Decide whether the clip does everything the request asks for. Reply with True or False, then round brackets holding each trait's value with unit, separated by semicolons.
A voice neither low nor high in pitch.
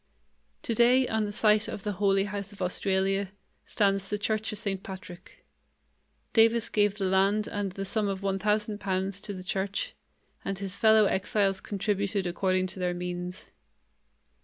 False (200 Hz)